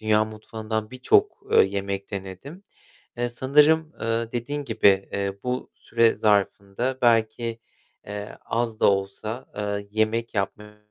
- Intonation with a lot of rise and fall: No, average, 2.9 semitones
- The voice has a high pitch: No, low, 110 Hz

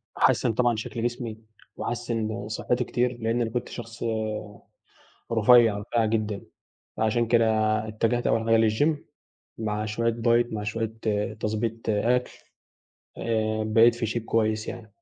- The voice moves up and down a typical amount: No, narrow, 1.5 semitones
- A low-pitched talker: Yes, low, 115 Hz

